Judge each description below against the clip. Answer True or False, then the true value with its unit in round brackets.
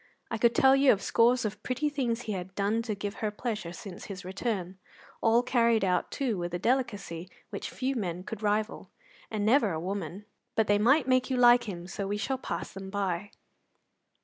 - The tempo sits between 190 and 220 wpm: True (200 wpm)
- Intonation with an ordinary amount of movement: True (3.9 semitones)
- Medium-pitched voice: False (210 Hz)